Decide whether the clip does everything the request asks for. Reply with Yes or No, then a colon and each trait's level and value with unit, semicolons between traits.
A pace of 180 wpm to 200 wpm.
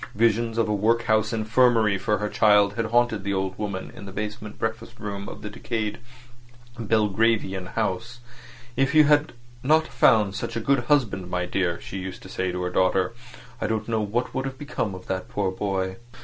Yes: average, 190 wpm